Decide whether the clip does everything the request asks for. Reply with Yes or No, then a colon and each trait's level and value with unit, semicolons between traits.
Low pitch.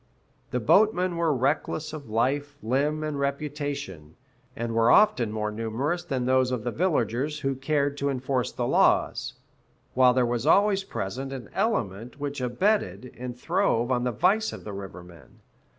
Yes: low, 130 Hz